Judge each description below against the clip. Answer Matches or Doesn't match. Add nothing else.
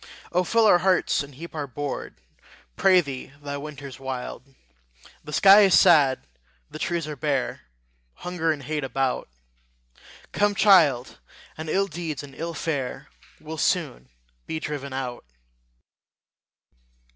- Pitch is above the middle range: Doesn't match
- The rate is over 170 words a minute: Doesn't match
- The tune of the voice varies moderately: Matches